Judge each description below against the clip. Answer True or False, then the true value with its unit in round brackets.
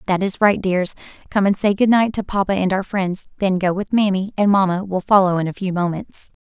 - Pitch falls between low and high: False (195 Hz)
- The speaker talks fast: True (245 wpm)